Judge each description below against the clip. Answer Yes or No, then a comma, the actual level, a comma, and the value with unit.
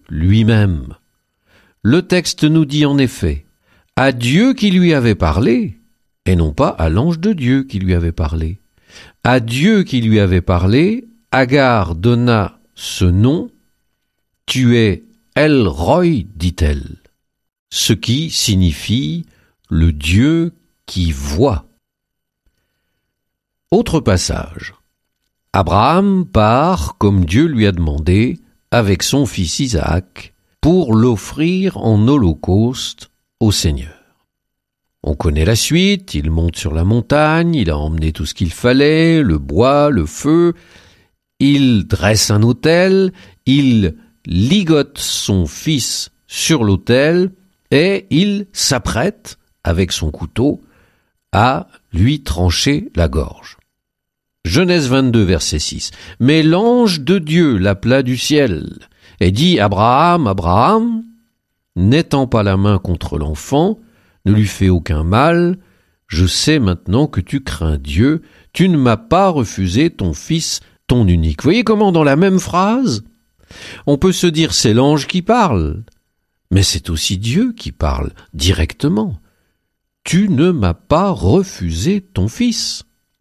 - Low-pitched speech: Yes, low, 110 Hz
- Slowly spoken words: Yes, slow, 125 wpm